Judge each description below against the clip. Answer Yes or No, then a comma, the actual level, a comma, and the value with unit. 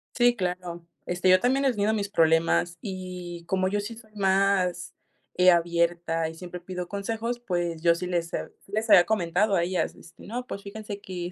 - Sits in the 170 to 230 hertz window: Yes, medium, 185 Hz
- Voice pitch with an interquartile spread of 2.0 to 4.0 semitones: Yes, average, 2.8 semitones